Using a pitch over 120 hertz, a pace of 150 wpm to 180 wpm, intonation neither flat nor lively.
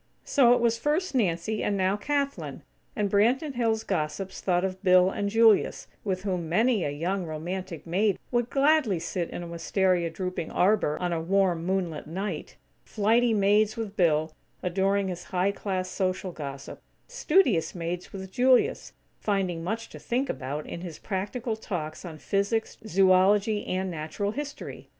Yes: high, 190 Hz; average, 160 wpm; average, 3.9 semitones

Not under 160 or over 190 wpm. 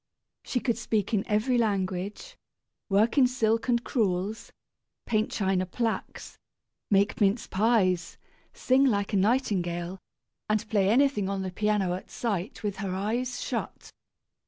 No: slow, 135 wpm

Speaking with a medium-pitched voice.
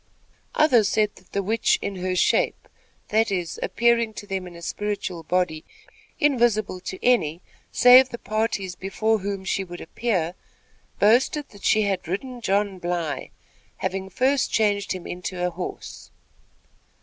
No: high, 200 Hz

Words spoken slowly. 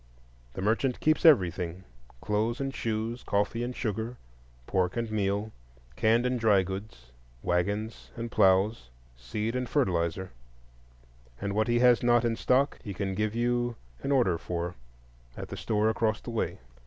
No: average, 145 wpm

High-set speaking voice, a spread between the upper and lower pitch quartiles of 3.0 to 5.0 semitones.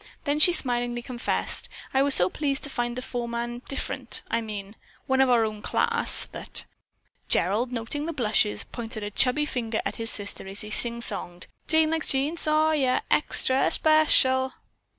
Yes: high, 245 Hz; average, 3.9 semitones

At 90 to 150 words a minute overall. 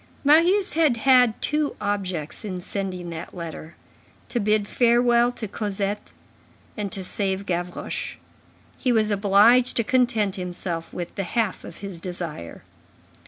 Yes: slow, 135 wpm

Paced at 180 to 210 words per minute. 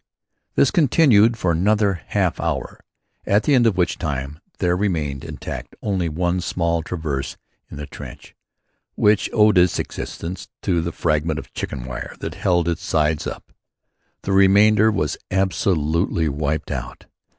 No: average, 150 wpm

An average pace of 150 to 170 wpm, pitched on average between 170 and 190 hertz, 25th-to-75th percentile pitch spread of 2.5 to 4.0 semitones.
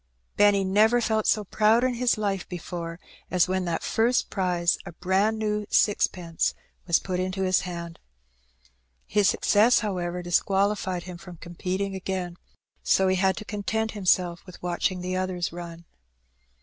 Yes: average, 160 wpm; medium, 185 Hz; average, 2.8 semitones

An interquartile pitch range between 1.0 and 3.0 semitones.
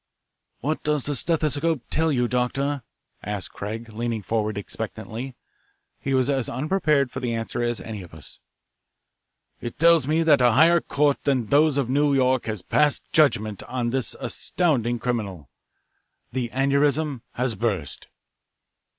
No: average, 4.2 semitones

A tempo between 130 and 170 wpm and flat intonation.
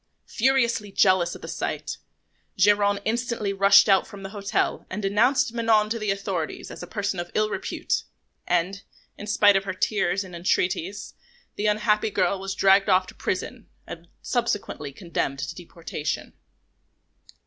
Yes: average, 155 wpm; narrow, 2.3 semitones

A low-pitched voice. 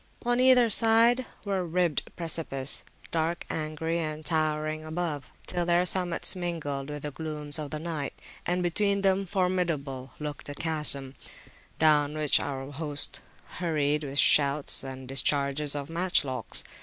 No: medium, 155 Hz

